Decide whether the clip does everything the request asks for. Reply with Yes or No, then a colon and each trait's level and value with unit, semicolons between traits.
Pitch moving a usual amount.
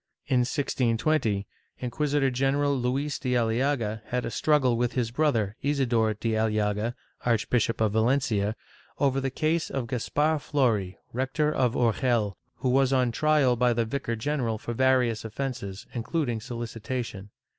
Yes: average, 3.3 semitones